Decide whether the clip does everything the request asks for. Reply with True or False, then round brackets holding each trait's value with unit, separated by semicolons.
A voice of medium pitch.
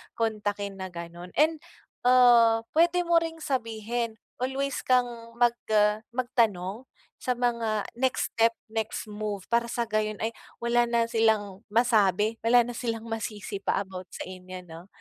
False (225 Hz)